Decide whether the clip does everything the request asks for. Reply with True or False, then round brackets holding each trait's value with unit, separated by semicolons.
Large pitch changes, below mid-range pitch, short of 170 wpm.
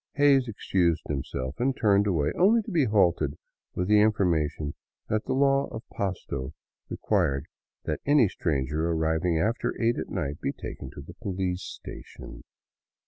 True (6.7 semitones; 95 Hz; 150 wpm)